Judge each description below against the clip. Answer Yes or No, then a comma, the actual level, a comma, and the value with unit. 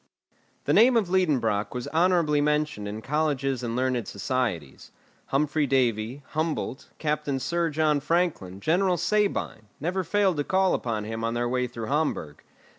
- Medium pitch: Yes, medium, 145 Hz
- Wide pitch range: Yes, wide, 5.9 semitones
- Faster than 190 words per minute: No, average, 150 wpm